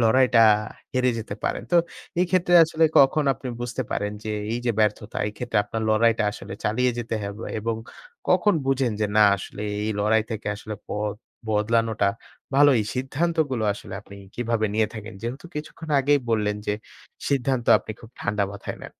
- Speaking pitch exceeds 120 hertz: No, low, 115 Hz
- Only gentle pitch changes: No, average, 3.7 semitones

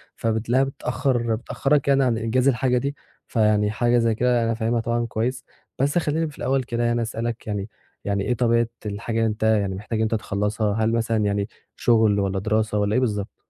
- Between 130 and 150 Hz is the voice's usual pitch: No, low, 115 Hz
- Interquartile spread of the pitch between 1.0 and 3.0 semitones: Yes, narrow, 2.4 semitones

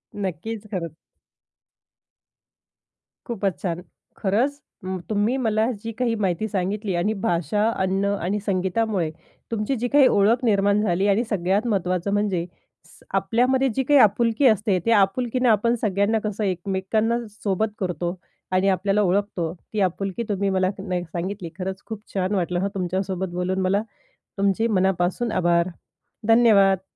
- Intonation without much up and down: No, average, 3.0 semitones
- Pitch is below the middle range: No, high, 200 Hz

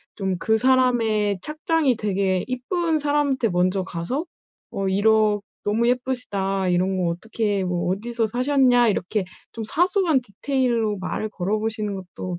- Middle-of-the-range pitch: No, high, 220 Hz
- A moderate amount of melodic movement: Yes, average, 4.8 semitones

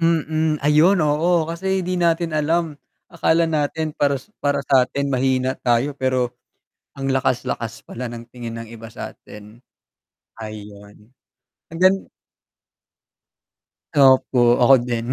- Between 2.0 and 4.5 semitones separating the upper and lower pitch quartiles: No, average, 5.0 semitones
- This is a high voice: No, medium, 140 Hz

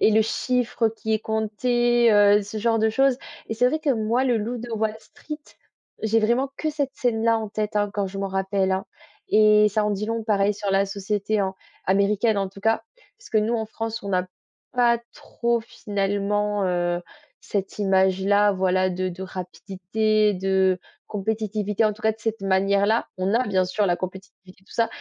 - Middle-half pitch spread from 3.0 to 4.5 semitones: No, narrow, 2.5 semitones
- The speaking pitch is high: Yes, high, 210 Hz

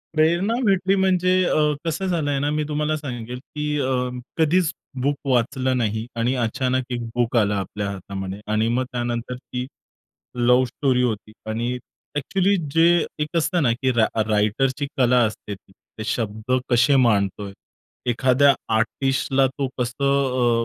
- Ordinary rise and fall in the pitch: Yes, average, 4.2 semitones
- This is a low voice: Yes, low, 130 Hz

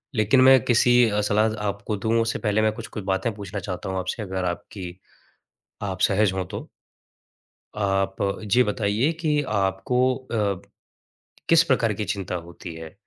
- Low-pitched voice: Yes, low, 105 Hz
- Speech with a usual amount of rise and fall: Yes, average, 3.2 semitones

